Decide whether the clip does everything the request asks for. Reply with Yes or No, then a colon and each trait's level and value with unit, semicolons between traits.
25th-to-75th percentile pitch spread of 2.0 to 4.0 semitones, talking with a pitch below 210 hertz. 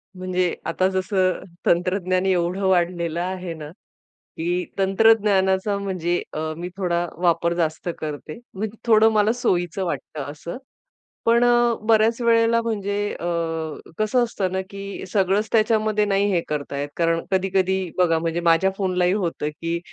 Yes: average, 3.2 semitones; medium, 185 Hz